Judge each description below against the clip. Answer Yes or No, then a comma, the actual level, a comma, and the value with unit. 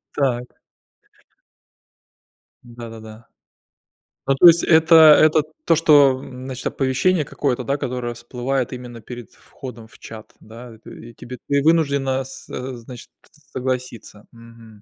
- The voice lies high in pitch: No, low, 125 Hz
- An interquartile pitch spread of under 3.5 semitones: Yes, average, 2.9 semitones